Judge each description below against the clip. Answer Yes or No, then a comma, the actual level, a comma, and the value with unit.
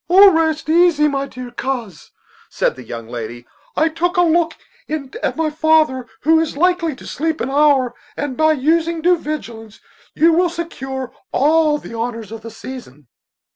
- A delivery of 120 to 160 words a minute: No, average, 175 wpm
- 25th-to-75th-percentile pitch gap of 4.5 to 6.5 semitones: Yes, average, 4.8 semitones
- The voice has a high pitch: Yes, very high, 300 Hz